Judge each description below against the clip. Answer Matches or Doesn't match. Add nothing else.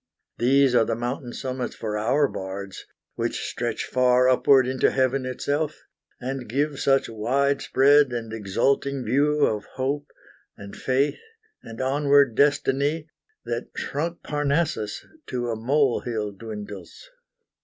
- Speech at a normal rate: Doesn't match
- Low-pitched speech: Matches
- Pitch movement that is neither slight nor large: Matches